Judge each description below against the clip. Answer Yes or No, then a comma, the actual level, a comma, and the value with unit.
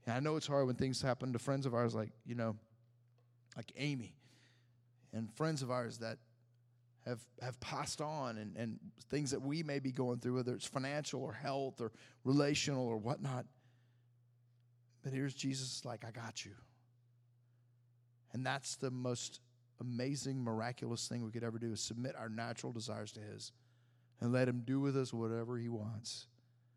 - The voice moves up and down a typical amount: No, narrow, 1.9 semitones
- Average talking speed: Yes, average, 175 wpm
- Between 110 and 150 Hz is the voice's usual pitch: Yes, low, 120 Hz